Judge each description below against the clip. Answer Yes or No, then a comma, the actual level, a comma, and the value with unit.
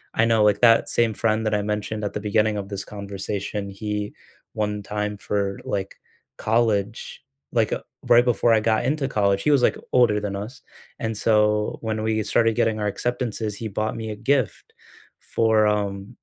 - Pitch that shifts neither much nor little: No, narrow, 1.6 semitones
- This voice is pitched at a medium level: No, low, 105 Hz